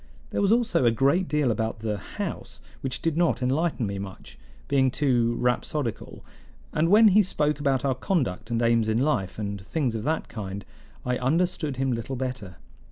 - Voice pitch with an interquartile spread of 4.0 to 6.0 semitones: Yes, average, 5.2 semitones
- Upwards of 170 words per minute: Yes, average, 180 wpm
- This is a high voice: No, low, 130 Hz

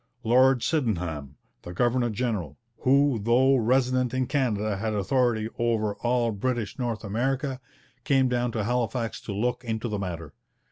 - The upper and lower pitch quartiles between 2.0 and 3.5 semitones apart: Yes, average, 3.2 semitones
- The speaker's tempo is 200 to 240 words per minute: No, average, 145 wpm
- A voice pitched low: Yes, low, 120 Hz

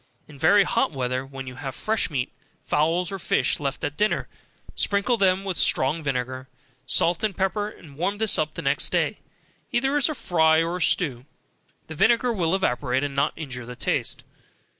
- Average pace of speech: Yes, average, 180 wpm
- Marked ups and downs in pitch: Yes, wide, 6.6 semitones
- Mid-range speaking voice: Yes, medium, 160 Hz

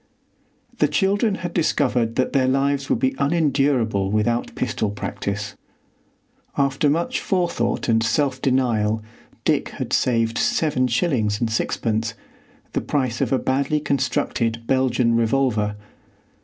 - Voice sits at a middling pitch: No, low, 130 Hz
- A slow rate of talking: Yes, slow, 125 wpm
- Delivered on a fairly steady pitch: No, average, 3.8 semitones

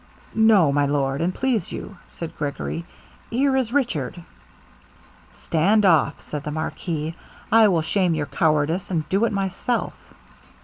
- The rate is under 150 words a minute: Yes, average, 140 wpm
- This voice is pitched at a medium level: Yes, medium, 170 Hz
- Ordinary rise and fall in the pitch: No, wide, 5.8 semitones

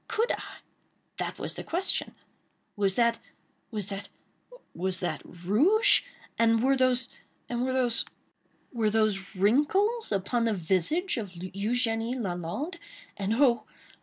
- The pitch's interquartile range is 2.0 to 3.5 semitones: No, average, 4.8 semitones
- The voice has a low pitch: No, high, 230 Hz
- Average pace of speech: No, slow, 105 wpm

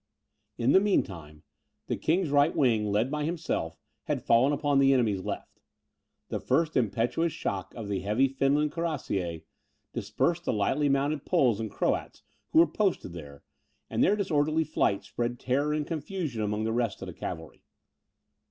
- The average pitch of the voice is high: No, low, 135 Hz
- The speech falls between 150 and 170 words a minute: Yes, average, 165 wpm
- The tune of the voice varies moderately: No, wide, 6.5 semitones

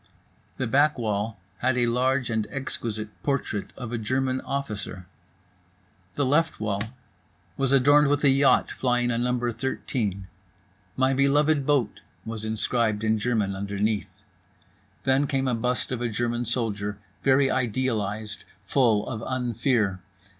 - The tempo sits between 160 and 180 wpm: No, slow, 135 wpm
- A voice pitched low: Yes, low, 120 Hz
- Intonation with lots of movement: No, average, 3.6 semitones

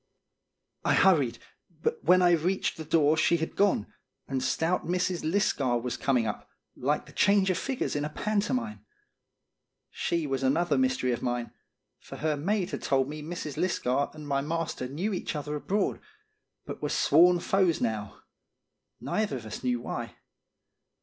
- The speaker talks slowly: No, average, 165 wpm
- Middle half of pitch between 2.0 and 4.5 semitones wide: No, average, 5.3 semitones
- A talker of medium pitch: Yes, medium, 155 Hz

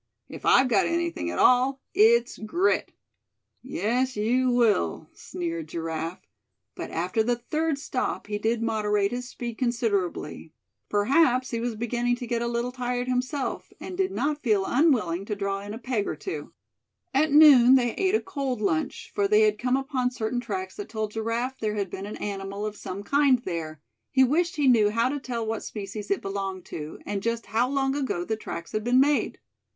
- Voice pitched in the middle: No, high, 235 Hz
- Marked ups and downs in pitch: No, average, 4.0 semitones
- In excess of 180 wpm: Yes, average, 190 wpm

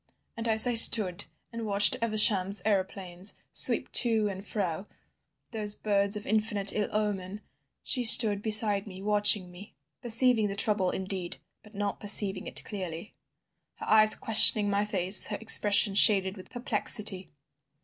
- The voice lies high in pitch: Yes, high, 205 Hz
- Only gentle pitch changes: Yes, narrow, 1.9 semitones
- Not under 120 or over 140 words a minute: Yes, slow, 135 wpm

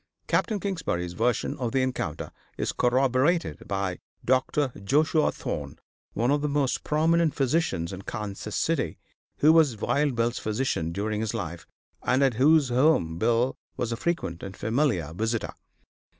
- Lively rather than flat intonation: Yes, wide, 6.1 semitones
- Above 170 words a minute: No, average, 150 wpm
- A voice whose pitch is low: Yes, low, 125 Hz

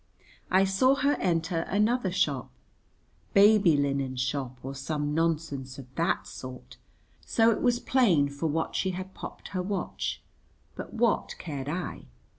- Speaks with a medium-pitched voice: Yes, medium, 165 Hz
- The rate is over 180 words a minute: No, average, 145 wpm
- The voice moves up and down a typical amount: No, wide, 6.1 semitones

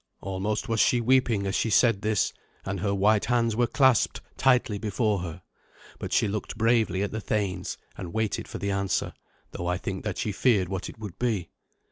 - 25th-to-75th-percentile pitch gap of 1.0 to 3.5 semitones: Yes, average, 2.8 semitones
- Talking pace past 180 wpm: Yes, average, 195 wpm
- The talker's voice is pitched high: No, low, 105 Hz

